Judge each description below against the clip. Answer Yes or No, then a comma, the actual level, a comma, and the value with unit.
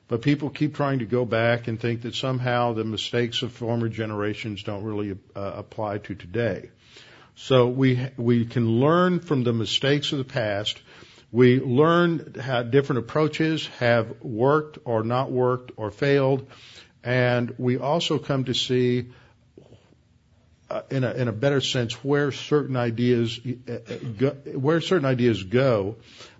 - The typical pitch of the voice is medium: No, low, 125 Hz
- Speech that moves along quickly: No, average, 150 wpm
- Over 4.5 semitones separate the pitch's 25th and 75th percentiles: No, average, 2.8 semitones